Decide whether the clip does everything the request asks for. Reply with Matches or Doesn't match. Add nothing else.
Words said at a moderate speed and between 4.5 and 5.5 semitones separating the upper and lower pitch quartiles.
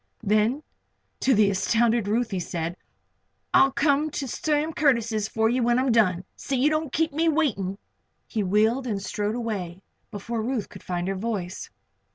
Matches